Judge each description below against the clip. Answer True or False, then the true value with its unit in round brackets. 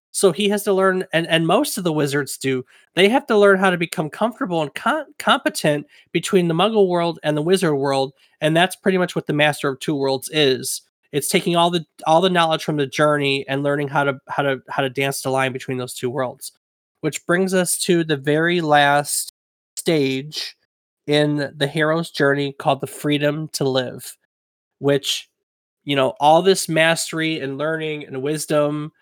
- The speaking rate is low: False (195 wpm)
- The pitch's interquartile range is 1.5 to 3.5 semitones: False (3.9 semitones)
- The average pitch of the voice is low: False (155 Hz)